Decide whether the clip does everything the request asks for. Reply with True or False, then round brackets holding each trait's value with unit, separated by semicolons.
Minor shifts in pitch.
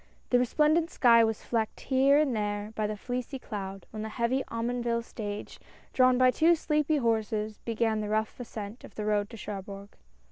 False (3.2 semitones)